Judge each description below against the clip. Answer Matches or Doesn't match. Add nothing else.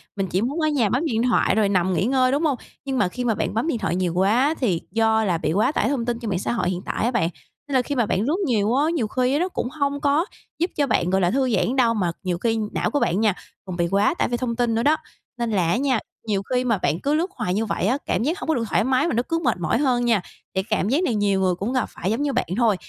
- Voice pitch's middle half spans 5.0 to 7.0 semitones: Matches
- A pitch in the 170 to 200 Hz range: Doesn't match